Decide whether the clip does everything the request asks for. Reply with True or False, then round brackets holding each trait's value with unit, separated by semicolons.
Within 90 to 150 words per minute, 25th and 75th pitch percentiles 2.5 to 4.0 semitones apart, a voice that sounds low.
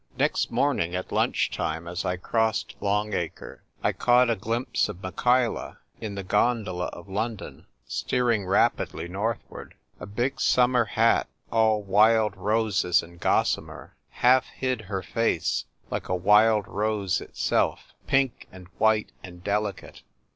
True (140 wpm; 3.6 semitones; 105 Hz)